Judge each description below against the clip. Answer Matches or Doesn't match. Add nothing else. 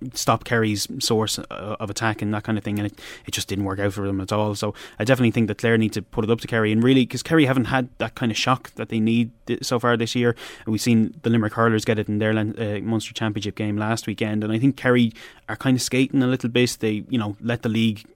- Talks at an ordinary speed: Doesn't match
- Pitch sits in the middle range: Doesn't match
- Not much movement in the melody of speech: Matches